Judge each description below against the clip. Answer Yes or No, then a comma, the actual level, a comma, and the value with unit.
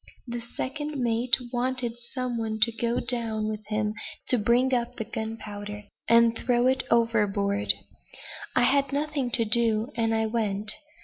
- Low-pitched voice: No, high, 235 Hz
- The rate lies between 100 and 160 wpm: Yes, average, 150 wpm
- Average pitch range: No, narrow, 2.2 semitones